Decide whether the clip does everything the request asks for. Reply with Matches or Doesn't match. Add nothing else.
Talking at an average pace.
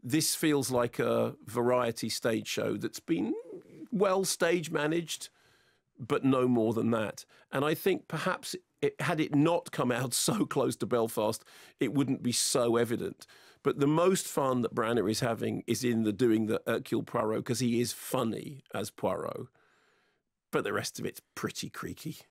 Matches